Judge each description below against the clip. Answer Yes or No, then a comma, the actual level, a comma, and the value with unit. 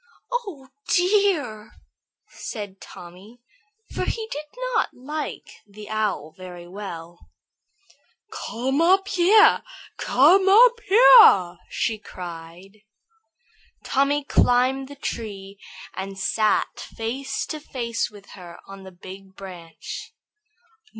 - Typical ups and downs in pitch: No, wide, 7.8 semitones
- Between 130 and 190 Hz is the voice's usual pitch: No, high, 220 Hz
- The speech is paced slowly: Yes, slow, 105 wpm